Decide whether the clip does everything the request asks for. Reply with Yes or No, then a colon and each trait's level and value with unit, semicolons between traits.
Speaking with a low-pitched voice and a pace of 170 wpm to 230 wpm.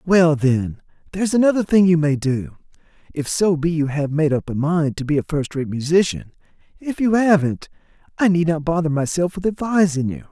No: medium, 160 Hz; average, 200 wpm